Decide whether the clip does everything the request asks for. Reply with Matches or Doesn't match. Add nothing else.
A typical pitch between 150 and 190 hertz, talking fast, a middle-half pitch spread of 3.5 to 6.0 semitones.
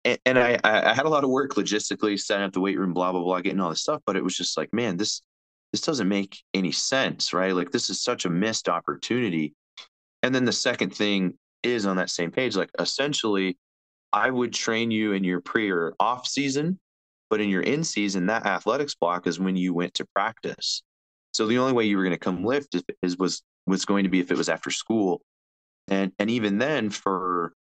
Doesn't match